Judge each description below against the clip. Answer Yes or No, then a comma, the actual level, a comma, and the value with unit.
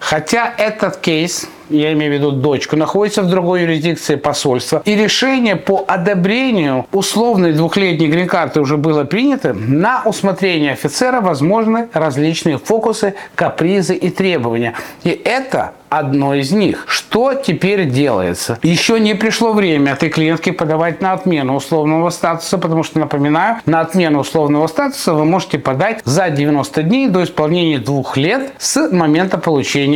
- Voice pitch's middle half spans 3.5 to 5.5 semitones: Yes, average, 4.6 semitones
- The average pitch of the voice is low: No, medium, 165 Hz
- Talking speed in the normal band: Yes, average, 140 wpm